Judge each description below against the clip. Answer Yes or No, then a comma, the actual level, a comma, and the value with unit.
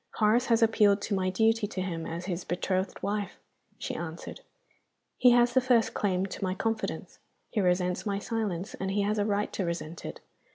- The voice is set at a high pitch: Yes, high, 200 Hz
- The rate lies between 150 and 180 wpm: No, average, 195 wpm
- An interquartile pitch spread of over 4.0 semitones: No, average, 3.2 semitones